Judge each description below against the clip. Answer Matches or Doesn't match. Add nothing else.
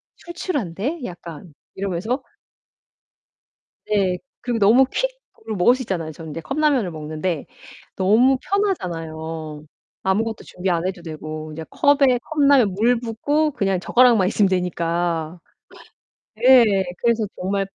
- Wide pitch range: Matches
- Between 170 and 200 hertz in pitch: Matches